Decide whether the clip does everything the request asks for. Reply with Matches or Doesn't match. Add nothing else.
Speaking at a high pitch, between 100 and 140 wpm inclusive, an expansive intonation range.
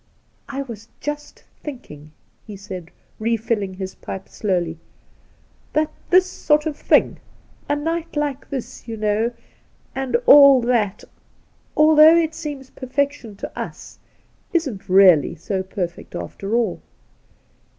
Matches